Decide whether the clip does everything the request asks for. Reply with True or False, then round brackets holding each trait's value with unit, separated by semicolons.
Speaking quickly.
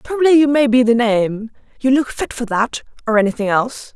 True (210 wpm)